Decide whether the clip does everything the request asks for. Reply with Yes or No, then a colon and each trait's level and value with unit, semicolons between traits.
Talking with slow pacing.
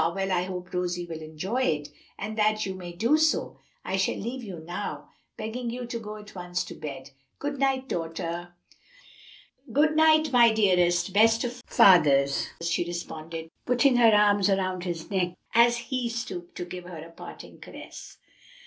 No: average, 170 wpm